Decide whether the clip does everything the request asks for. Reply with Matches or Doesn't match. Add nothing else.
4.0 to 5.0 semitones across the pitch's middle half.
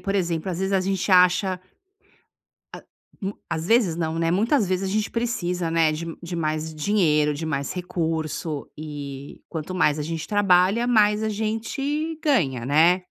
Matches